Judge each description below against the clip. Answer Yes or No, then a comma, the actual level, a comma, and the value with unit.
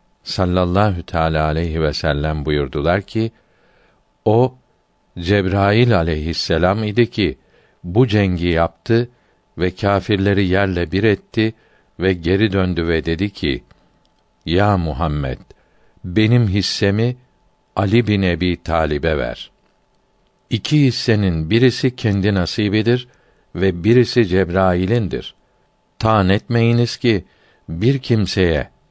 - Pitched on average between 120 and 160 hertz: No, low, 100 Hz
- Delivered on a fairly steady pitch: No, average, 4.5 semitones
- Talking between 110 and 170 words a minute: No, average, 100 wpm